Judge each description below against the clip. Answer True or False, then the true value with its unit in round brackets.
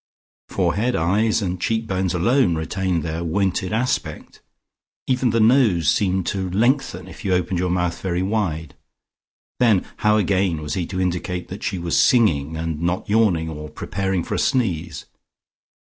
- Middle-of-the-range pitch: False (95 Hz)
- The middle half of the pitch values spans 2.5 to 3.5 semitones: False (3.9 semitones)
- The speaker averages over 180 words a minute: False (160 wpm)